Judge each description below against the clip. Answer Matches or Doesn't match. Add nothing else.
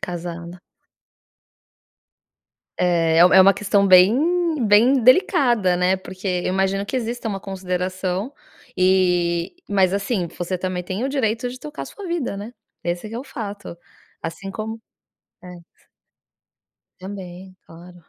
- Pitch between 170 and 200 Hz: Matches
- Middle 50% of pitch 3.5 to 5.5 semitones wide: Matches